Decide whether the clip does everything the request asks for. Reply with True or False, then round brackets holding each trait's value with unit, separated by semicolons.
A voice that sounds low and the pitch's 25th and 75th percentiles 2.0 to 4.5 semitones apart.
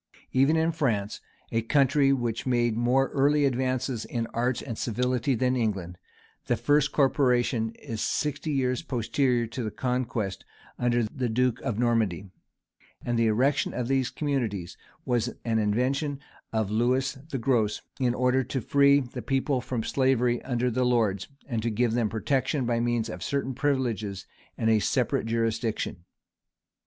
True (125 Hz; 2.8 semitones)